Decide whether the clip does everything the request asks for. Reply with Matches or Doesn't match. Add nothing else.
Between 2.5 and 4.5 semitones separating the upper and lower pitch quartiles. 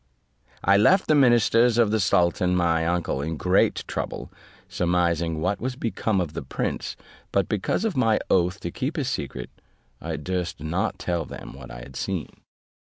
Doesn't match